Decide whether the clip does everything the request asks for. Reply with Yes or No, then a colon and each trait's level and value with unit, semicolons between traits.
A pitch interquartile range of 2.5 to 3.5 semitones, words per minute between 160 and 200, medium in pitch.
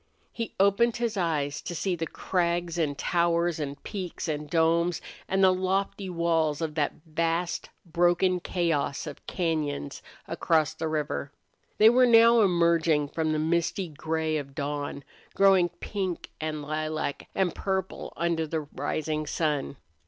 No: average, 2.9 semitones; average, 145 wpm; medium, 165 Hz